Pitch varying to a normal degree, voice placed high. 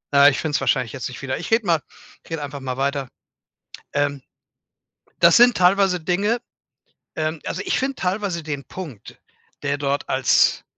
No: average, 4.8 semitones; medium, 155 Hz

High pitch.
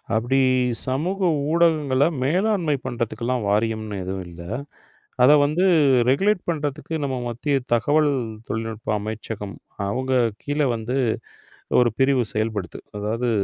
No: low, 130 Hz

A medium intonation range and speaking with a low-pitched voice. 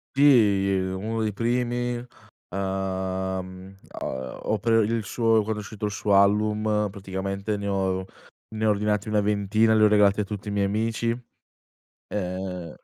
No: narrow, 2.1 semitones; low, 105 Hz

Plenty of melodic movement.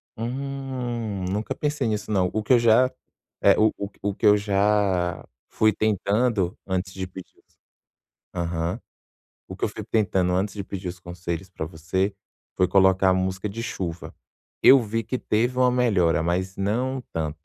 No: average, 3.8 semitones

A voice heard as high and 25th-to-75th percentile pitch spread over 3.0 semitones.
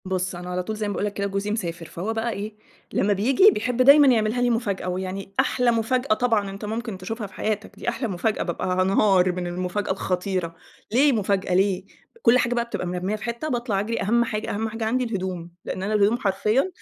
Yes: high, 210 Hz; average, 3.7 semitones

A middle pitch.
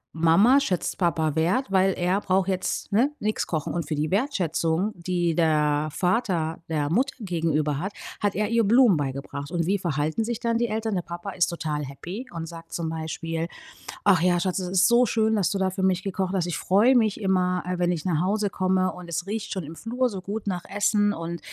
Yes: medium, 180 Hz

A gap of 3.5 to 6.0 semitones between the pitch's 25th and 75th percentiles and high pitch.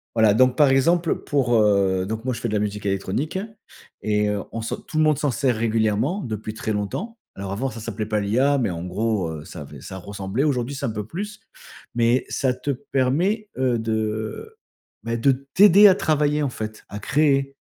No: average, 5.2 semitones; low, 115 Hz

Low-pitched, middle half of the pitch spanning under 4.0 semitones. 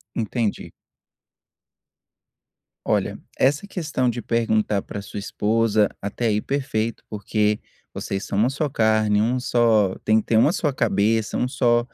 Yes: low, 110 Hz; average, 2.8 semitones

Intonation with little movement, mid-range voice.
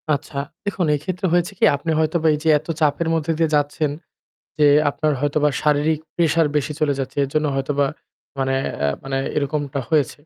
Yes: narrow, 2.1 semitones; medium, 150 Hz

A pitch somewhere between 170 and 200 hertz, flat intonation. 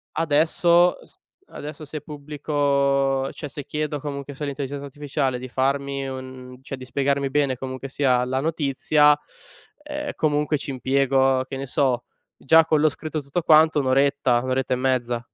No: medium, 140 Hz; narrow, 2.0 semitones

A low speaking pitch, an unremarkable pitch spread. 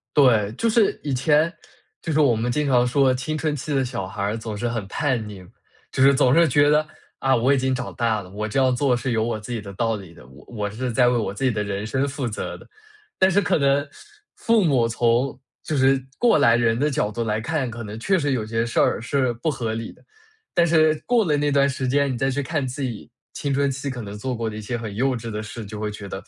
Yes: low, 125 Hz; average, 4.2 semitones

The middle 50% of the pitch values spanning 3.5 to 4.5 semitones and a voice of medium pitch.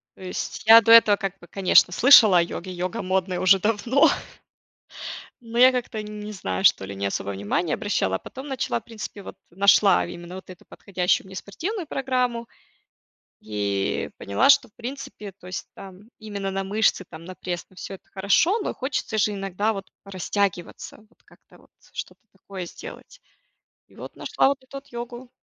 No: average, 4.2 semitones; high, 200 Hz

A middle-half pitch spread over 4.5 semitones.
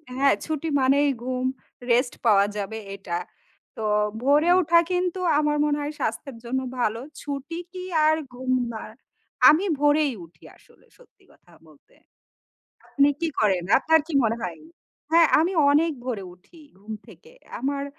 Yes: average, 5.2 semitones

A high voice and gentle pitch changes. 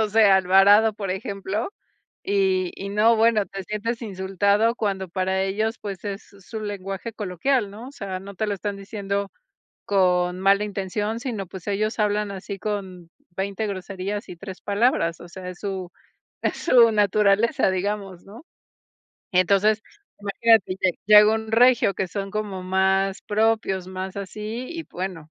Yes: high, 200 Hz; narrow, 2.2 semitones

